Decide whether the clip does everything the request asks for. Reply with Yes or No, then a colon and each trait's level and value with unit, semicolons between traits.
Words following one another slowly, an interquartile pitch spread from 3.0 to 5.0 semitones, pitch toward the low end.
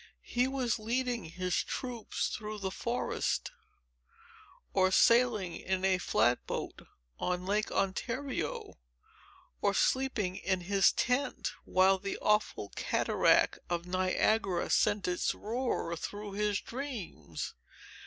No: slow, 115 wpm; average, 4.4 semitones; high, 205 Hz